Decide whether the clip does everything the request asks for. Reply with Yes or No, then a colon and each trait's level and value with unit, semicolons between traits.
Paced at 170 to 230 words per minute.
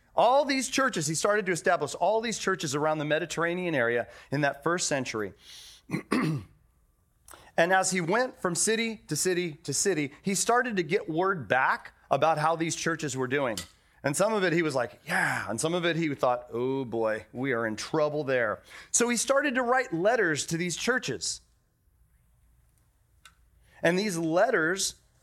Yes: average, 175 wpm